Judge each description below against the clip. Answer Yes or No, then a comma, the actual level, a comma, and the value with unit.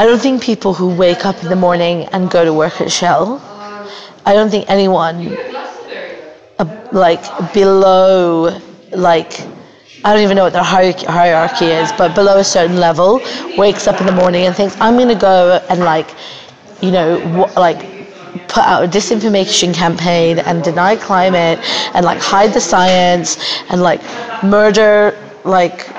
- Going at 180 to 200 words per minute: No, average, 160 wpm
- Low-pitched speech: No, medium, 185 Hz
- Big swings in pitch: No, average, 2.7 semitones